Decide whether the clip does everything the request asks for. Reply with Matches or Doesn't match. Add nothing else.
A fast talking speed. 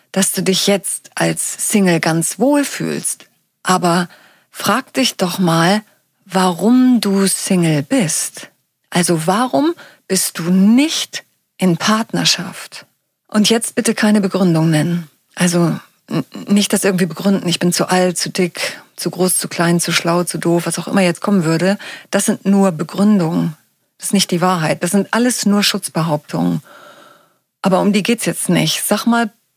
Doesn't match